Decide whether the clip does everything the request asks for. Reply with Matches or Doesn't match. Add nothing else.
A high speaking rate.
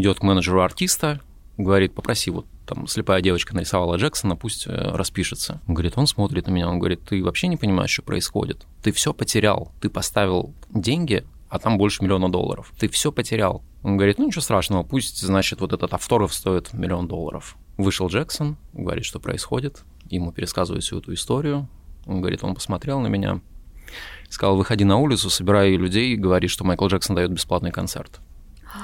Matches